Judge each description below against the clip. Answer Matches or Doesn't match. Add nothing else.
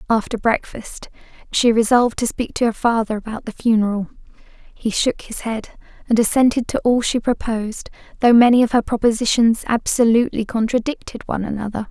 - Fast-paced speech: Doesn't match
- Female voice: Matches